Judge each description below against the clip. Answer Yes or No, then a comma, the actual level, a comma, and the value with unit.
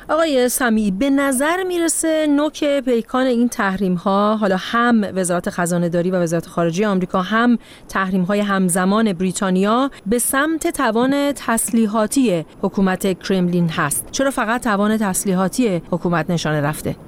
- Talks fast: No, average, 135 wpm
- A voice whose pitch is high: Yes, high, 205 Hz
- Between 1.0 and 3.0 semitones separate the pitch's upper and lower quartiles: No, average, 5.0 semitones